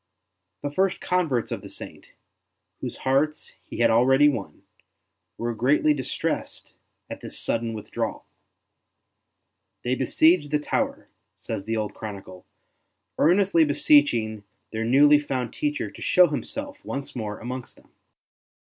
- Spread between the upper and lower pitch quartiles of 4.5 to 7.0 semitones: Yes, average, 5.0 semitones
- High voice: No, low, 135 Hz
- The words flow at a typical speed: No, slow, 130 wpm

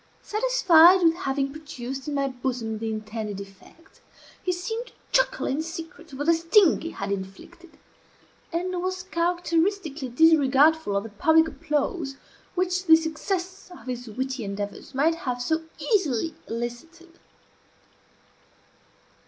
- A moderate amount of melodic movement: No, wide, 5.8 semitones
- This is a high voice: Yes, very high, 320 Hz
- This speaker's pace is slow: Yes, slow, 130 wpm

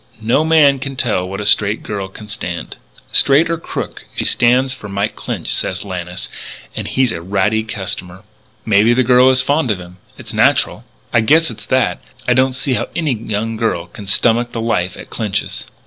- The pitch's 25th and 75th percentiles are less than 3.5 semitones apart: No, average, 4.8 semitones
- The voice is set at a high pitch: No, low, 110 Hz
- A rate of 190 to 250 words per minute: Yes, average, 195 wpm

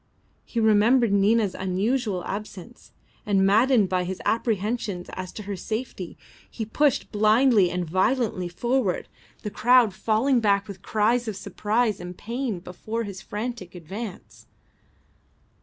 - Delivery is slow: Yes, slow, 130 wpm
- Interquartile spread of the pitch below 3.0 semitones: No, average, 3.7 semitones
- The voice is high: Yes, high, 210 Hz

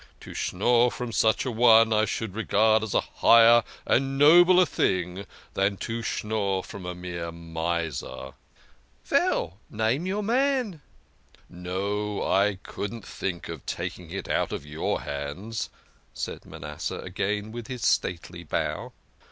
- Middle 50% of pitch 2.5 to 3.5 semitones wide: No, average, 4.7 semitones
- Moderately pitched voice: No, low, 105 Hz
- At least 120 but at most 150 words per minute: Yes, average, 140 wpm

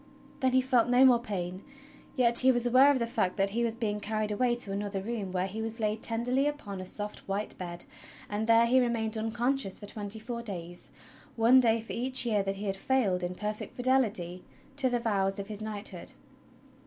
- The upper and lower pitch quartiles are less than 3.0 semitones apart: No, average, 3.4 semitones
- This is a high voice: Yes, high, 220 Hz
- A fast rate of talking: Yes, fast, 215 wpm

